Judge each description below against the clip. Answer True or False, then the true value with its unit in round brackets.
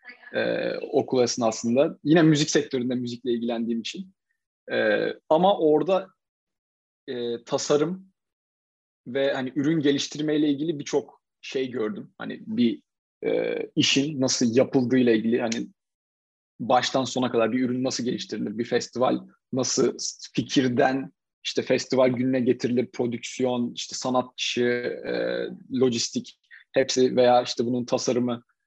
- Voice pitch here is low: True (130 Hz)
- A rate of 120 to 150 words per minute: False (110 wpm)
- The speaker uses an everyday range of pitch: True (4.5 semitones)